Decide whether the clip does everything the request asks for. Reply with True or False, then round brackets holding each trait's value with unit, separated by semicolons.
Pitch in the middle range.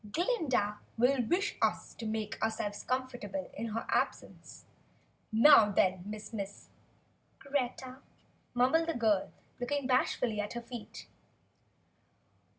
False (240 Hz)